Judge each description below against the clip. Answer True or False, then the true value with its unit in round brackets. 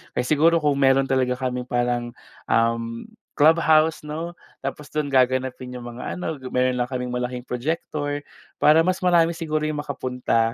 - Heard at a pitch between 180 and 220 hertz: False (130 Hz)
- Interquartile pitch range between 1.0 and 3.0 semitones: False (3.7 semitones)